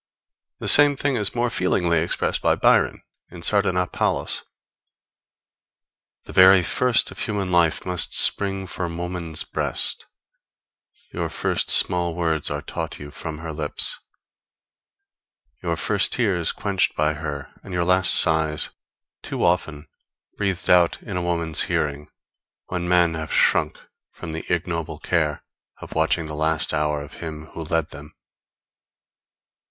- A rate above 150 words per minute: No, slow, 135 wpm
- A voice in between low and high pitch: No, very low, 85 Hz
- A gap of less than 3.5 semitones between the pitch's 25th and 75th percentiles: Yes, average, 2.7 semitones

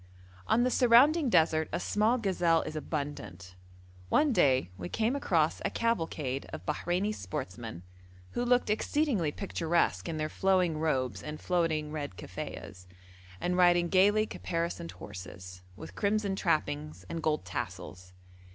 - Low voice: No, medium, 165 Hz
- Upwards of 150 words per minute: No, slow, 135 wpm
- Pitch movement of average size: No, wide, 6.5 semitones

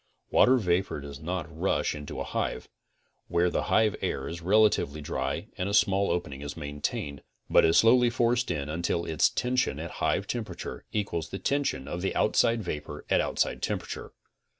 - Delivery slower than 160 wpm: No, average, 175 wpm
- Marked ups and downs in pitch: Yes, wide, 6.3 semitones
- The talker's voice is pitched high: No, very low, 85 Hz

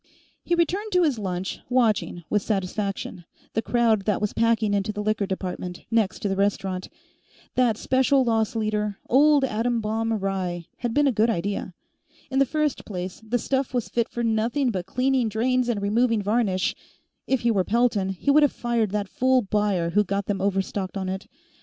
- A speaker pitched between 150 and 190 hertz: No, high, 215 Hz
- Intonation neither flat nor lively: Yes, average, 3.8 semitones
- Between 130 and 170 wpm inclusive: No, average, 185 wpm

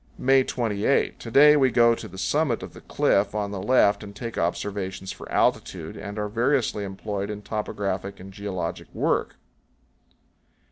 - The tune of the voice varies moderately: Yes, average, 3.1 semitones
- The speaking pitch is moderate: No, low, 105 Hz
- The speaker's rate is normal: Yes, average, 160 wpm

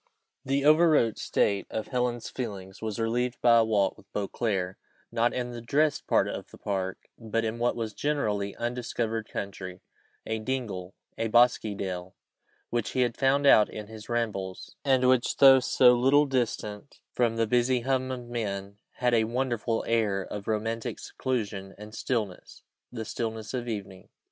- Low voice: Yes, low, 115 Hz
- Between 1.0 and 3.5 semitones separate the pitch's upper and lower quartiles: Yes, average, 3.1 semitones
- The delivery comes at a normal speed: Yes, average, 165 wpm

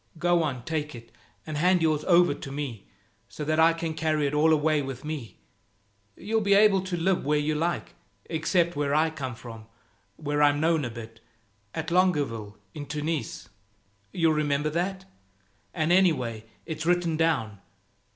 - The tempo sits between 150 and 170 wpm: Yes, average, 165 wpm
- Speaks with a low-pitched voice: No, medium, 155 Hz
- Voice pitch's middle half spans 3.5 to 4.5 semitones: No, average, 2.9 semitones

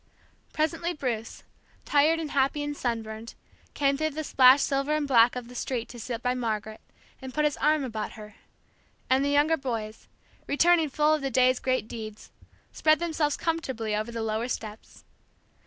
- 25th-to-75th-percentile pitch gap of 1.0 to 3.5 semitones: No, average, 4.6 semitones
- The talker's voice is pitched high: Yes, very high, 260 Hz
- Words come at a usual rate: Yes, average, 170 wpm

